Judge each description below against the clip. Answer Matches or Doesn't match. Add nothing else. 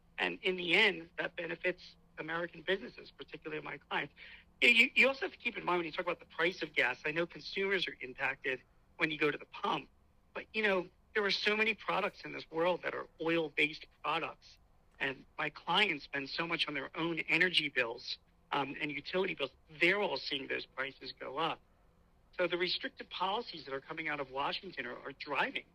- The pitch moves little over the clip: Doesn't match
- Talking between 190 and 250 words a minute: Matches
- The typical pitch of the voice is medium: Matches